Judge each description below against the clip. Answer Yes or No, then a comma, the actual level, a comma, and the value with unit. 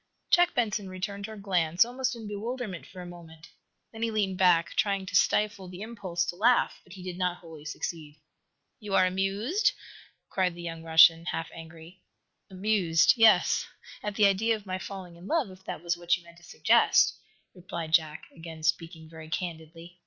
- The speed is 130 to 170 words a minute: No, average, 180 wpm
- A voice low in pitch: No, medium, 185 Hz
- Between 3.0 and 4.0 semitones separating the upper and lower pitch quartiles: Yes, average, 3.7 semitones